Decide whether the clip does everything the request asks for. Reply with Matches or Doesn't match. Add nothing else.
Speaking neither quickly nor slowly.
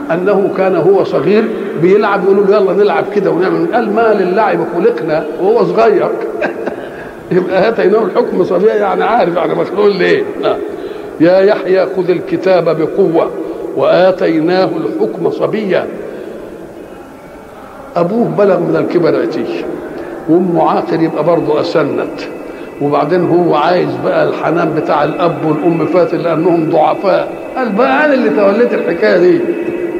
Matches